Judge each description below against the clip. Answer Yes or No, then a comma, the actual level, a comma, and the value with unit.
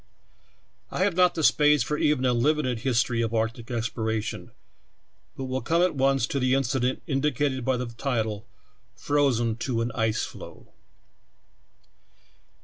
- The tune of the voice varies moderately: Yes, average, 3.7 semitones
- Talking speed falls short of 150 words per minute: Yes, average, 140 wpm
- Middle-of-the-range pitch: No, low, 130 Hz